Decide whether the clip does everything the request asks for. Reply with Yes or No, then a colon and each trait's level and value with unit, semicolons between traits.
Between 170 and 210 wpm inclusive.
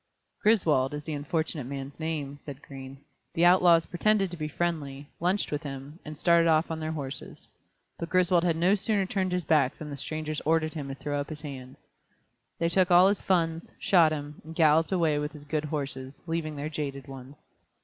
Yes: average, 200 wpm